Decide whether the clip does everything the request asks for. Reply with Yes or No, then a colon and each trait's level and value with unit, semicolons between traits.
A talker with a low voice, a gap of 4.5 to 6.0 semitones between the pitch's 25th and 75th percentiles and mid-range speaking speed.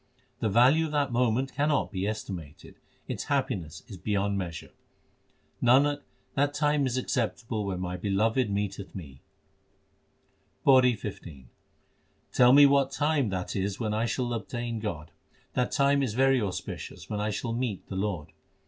Yes: low, 115 Hz; average, 5.3 semitones; average, 150 wpm